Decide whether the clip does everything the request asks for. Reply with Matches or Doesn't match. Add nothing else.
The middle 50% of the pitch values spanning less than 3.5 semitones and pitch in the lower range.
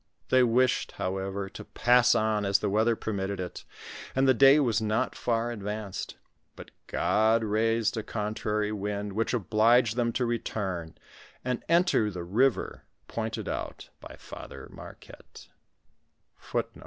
Matches